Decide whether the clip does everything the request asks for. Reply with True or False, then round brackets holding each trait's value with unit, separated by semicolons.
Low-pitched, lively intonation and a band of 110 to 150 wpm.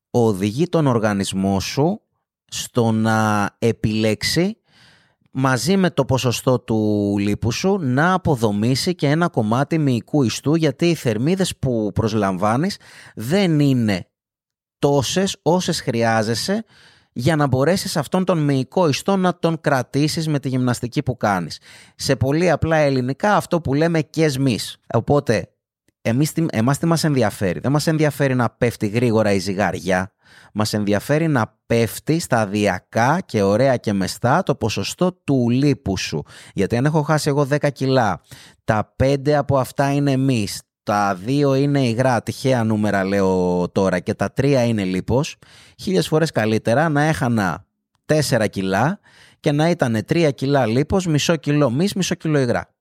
True (130 Hz; 5.7 semitones; 145 wpm)